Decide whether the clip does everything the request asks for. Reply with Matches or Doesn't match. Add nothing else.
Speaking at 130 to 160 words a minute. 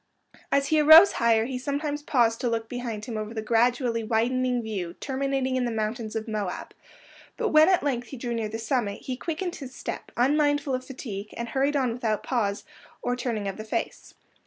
Doesn't match